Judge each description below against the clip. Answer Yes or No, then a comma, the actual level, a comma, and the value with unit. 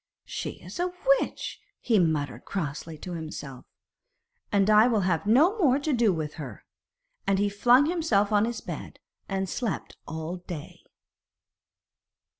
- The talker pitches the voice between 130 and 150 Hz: No, high, 200 Hz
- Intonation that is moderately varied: No, wide, 7.0 semitones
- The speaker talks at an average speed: Yes, average, 145 wpm